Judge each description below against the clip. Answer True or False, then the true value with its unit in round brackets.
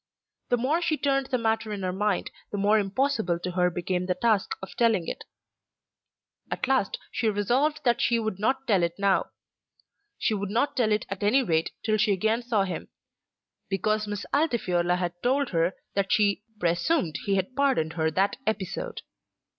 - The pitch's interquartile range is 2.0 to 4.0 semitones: False (4.7 semitones)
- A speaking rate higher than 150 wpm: True (180 wpm)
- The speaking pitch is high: True (210 Hz)